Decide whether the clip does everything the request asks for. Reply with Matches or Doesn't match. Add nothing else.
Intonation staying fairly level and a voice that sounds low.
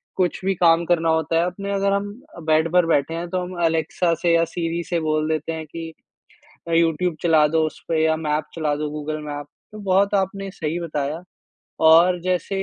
Doesn't match